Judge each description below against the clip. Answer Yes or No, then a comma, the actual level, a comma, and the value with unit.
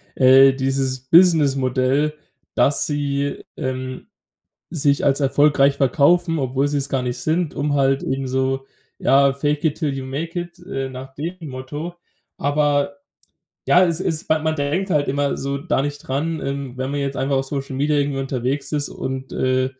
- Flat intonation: Yes, narrow, 2.0 semitones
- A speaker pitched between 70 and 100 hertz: No, medium, 140 Hz